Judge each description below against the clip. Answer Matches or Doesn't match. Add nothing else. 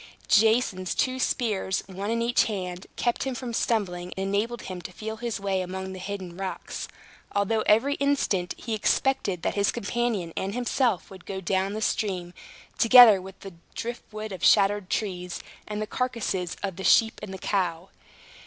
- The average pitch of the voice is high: Matches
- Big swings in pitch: Doesn't match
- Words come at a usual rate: Matches